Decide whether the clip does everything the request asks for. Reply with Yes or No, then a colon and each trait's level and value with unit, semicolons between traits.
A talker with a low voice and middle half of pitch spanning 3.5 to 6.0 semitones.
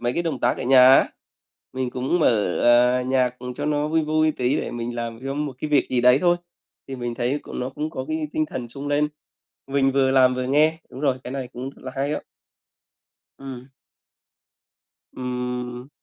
No: low, 130 Hz; average, 2.8 semitones